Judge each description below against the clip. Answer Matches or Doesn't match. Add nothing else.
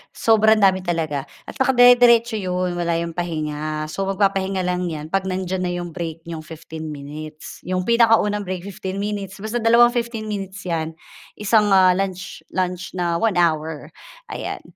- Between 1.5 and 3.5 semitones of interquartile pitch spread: Doesn't match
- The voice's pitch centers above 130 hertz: Matches